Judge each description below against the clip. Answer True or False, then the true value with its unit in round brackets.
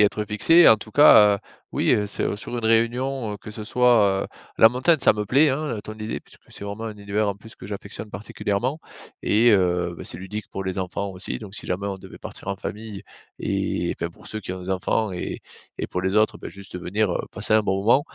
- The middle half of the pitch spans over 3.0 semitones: False (2.5 semitones)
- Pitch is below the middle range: True (105 Hz)